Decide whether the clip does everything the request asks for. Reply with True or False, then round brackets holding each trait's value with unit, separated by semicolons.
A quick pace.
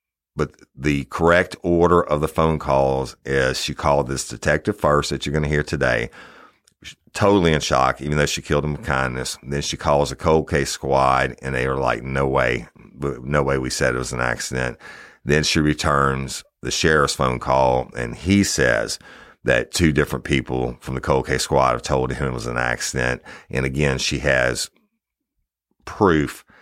False (190 wpm)